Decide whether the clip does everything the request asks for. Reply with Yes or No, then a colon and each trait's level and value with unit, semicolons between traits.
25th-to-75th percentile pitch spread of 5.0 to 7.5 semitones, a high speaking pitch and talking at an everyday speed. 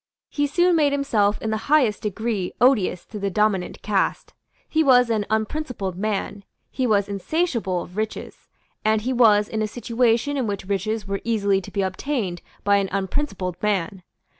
No: average, 3.9 semitones; high, 215 Hz; average, 170 wpm